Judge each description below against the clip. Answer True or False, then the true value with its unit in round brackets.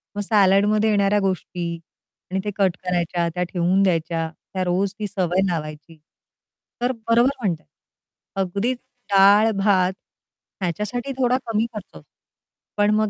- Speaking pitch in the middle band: False (195 Hz)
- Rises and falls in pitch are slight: False (3.0 semitones)